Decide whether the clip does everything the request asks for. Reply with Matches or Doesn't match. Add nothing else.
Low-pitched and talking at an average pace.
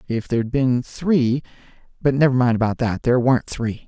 Matches